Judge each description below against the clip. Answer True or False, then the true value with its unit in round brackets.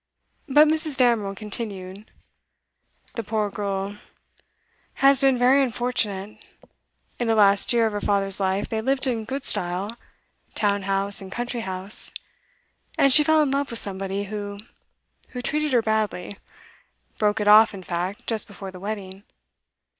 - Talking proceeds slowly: False (150 wpm)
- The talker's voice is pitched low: False (210 Hz)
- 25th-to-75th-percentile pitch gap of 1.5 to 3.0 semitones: False (3.8 semitones)